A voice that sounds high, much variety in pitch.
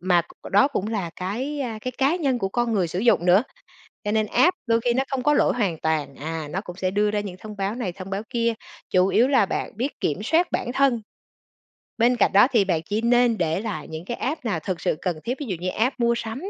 No: high, 215 Hz; average, 5.0 semitones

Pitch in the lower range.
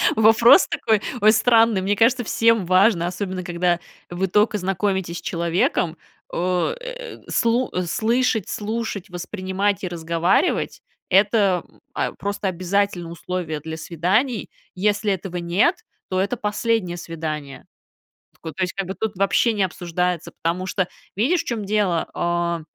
No: high, 190 Hz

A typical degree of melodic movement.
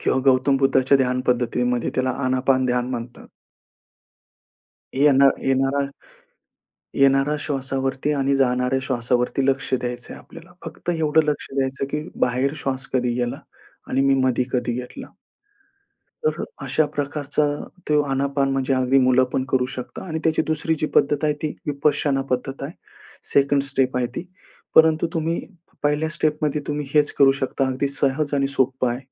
No: narrow, 2.2 semitones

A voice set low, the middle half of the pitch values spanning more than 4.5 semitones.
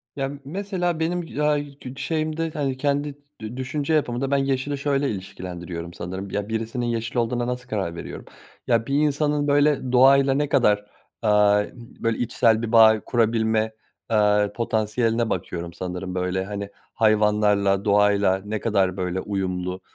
Yes: low, 115 Hz; average, 5.2 semitones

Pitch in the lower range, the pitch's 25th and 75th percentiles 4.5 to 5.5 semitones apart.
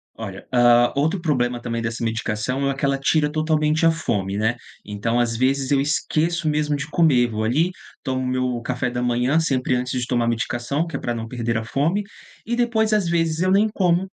Yes: low, 130 Hz; average, 4.9 semitones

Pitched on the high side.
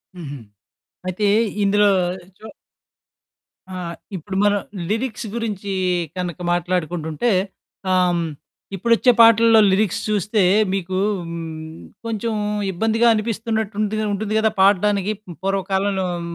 Yes: high, 200 Hz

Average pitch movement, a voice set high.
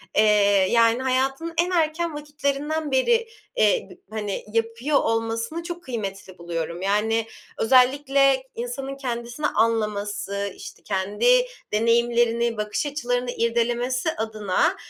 Yes: average, 4.8 semitones; high, 240 Hz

